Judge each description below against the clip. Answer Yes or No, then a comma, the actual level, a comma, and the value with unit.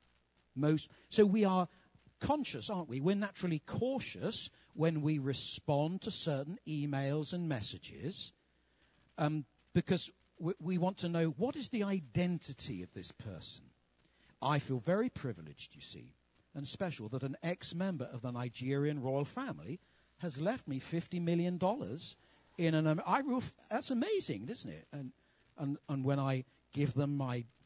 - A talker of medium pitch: Yes, medium, 150 Hz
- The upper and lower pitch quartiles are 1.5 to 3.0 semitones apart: No, average, 5.3 semitones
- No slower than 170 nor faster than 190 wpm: No, average, 150 wpm